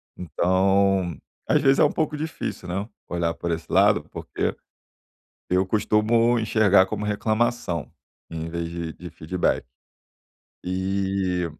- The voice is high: No, very low, 95 Hz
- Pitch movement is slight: No, average, 3.7 semitones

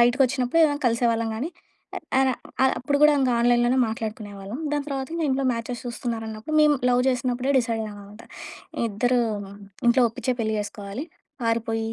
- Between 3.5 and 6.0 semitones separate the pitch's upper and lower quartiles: No, average, 2.8 semitones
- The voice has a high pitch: Yes, high, 240 Hz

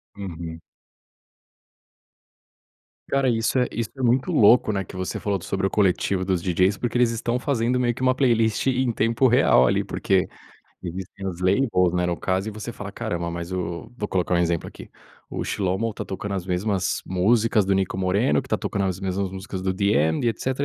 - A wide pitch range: No, average, 4.0 semitones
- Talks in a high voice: No, low, 100 Hz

